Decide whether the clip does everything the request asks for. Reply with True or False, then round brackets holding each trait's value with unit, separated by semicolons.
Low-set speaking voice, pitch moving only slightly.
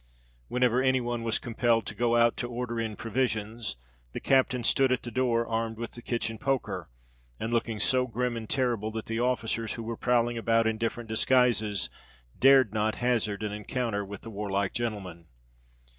True (115 Hz; 2.0 semitones)